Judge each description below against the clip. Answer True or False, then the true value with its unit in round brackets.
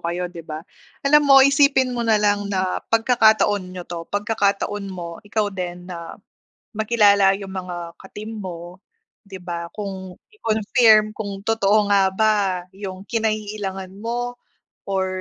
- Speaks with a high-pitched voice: True (200 Hz)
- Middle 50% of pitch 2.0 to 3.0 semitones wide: True (2.7 semitones)